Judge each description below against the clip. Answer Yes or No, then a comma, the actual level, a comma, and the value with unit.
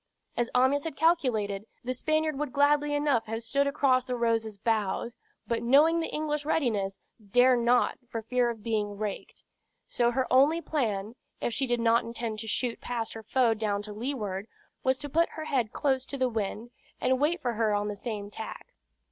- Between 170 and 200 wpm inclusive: Yes, average, 190 wpm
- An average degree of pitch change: Yes, average, 4.1 semitones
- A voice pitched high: Yes, high, 240 Hz